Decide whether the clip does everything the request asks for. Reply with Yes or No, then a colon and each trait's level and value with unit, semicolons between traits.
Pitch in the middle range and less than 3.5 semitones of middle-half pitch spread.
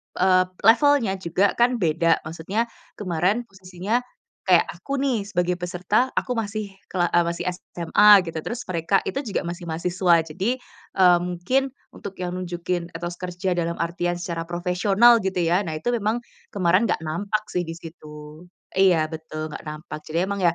Yes: medium, 180 Hz; average, 3.0 semitones